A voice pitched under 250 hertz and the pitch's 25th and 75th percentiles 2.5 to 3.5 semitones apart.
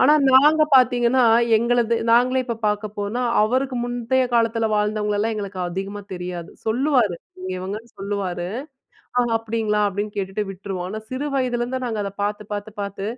Yes: high, 215 Hz; average, 3.2 semitones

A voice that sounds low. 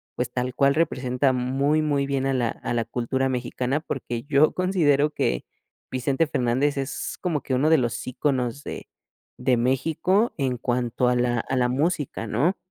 Yes: low, 130 Hz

